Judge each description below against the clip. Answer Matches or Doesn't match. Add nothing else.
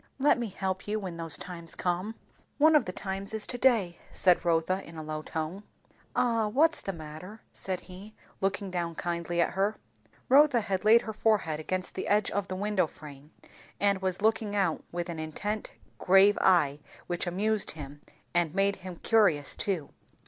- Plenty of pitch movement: Doesn't match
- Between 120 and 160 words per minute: Doesn't match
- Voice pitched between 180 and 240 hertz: Matches